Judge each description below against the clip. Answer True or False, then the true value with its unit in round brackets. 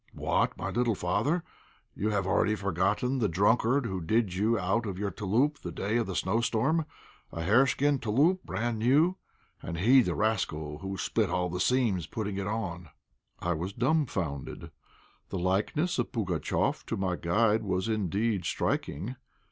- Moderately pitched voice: False (105 Hz)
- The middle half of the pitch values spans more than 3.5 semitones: True (4.6 semitones)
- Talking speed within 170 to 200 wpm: False (160 wpm)